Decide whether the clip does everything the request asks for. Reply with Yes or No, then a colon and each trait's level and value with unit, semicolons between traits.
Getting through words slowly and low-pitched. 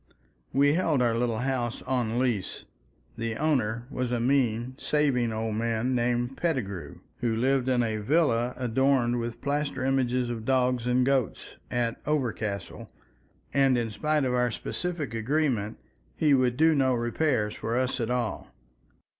No: average, 150 wpm; low, 125 Hz